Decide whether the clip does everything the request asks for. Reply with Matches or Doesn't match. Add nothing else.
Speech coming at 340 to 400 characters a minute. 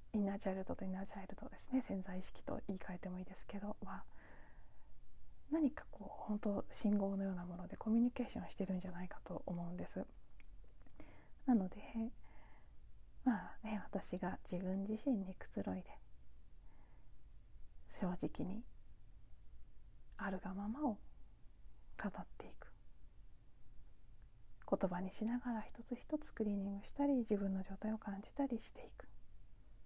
Doesn't match